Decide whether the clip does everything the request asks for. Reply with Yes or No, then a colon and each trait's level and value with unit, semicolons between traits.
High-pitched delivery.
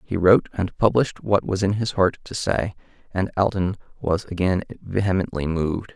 No: very low, 95 Hz